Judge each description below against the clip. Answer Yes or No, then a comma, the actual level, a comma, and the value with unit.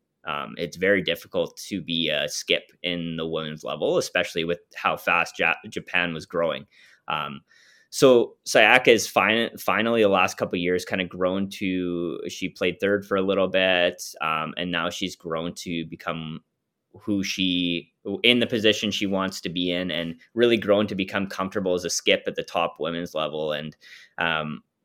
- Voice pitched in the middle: No, very low, 90 Hz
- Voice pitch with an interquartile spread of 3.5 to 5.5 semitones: No, average, 2.7 semitones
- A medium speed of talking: Yes, average, 180 wpm